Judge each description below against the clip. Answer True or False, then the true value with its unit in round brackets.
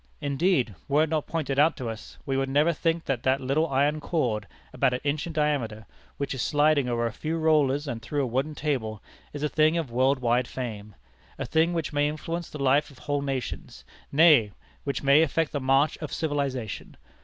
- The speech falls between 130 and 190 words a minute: False (205 wpm)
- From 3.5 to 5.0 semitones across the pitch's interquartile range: False (3.0 semitones)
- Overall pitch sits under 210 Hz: True (140 Hz)